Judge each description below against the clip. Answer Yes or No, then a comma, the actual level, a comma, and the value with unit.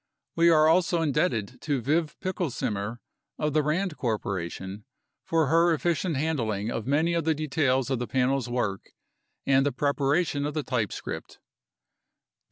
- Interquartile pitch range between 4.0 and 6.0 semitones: Yes, average, 4.9 semitones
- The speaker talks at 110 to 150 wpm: Yes, average, 145 wpm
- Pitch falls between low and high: Yes, medium, 145 Hz